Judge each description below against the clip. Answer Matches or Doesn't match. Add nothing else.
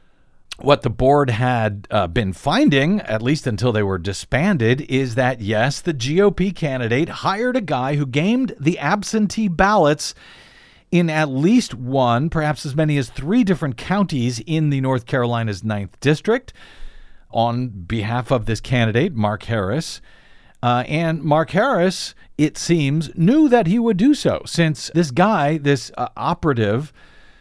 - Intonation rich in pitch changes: Matches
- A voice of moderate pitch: Matches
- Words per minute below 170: Matches